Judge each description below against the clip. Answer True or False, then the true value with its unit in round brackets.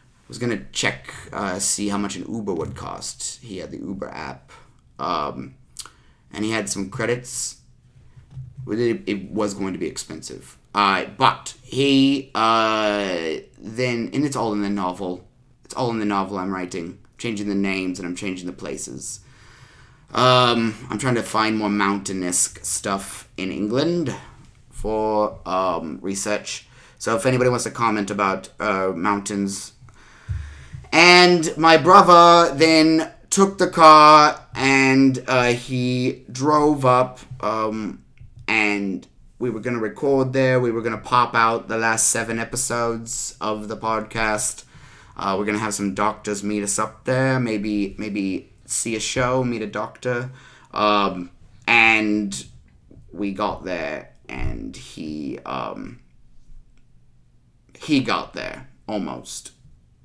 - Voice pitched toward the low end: True (110 Hz)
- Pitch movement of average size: True (3.9 semitones)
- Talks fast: False (140 wpm)